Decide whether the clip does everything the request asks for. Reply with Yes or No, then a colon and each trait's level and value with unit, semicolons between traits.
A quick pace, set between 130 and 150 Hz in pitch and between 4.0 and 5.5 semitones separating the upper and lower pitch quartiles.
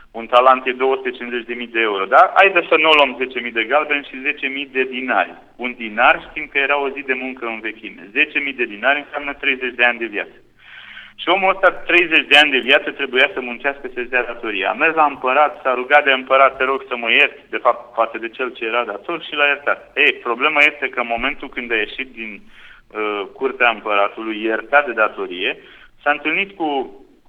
No: fast, 210 wpm; low, 135 Hz; average, 3.5 semitones